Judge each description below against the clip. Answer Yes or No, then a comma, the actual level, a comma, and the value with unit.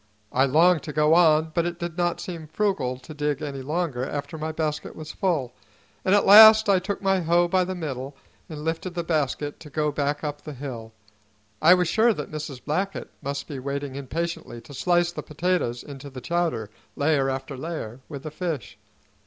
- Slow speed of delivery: No, average, 195 wpm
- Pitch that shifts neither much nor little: Yes, average, 3.7 semitones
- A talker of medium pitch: Yes, medium, 155 Hz